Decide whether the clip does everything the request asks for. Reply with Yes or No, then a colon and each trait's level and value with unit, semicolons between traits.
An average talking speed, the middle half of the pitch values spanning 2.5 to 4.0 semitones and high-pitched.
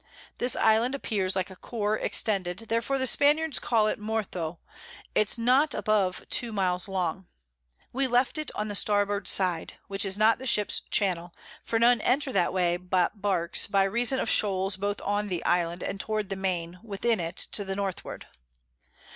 Yes: average, 175 wpm; average, 3.6 semitones; high, 205 Hz